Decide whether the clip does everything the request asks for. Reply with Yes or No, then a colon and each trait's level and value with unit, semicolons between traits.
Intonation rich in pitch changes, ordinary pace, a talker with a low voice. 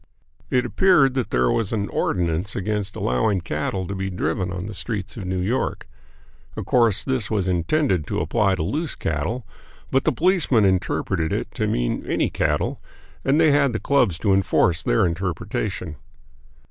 Yes: wide, 5.8 semitones; average, 170 wpm; low, 100 Hz